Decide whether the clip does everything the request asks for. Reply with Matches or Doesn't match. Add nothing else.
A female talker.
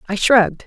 Matches